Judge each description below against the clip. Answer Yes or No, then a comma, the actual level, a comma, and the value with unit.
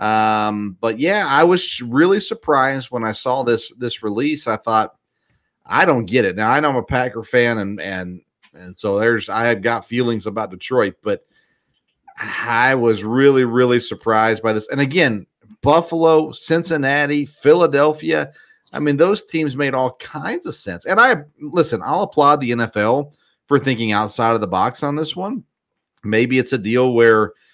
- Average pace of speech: Yes, average, 175 wpm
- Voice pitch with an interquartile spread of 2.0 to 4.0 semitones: No, average, 4.9 semitones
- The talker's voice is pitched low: Yes, low, 125 Hz